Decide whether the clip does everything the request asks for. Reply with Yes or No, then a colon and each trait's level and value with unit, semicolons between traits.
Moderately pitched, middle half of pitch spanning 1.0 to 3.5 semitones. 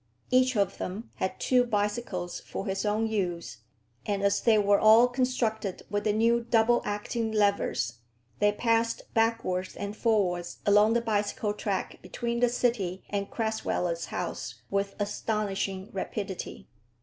No: high, 210 Hz; narrow, 2.5 semitones